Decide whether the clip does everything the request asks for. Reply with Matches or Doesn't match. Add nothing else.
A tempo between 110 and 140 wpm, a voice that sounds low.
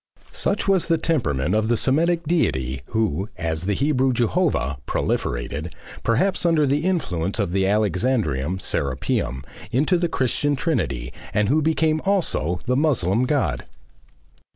Matches